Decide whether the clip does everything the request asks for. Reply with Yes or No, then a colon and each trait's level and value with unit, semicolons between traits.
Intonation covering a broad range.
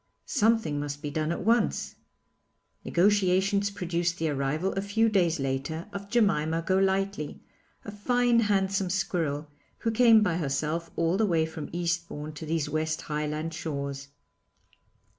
No: average, 4.5 semitones